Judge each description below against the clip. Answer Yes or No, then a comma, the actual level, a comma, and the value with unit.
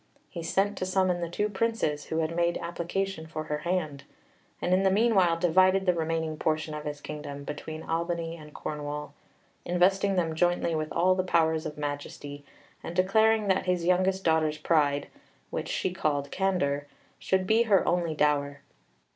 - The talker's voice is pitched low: No, medium, 170 Hz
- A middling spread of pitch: Yes, average, 3.5 semitones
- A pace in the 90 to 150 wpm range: No, average, 170 wpm